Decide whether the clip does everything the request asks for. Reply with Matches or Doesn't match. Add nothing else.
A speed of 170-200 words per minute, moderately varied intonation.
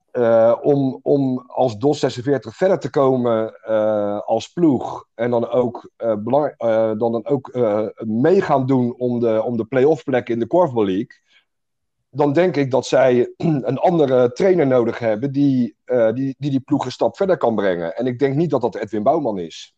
Matches